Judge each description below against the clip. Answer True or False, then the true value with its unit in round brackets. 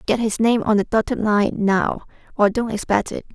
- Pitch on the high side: True (215 Hz)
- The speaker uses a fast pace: True (215 wpm)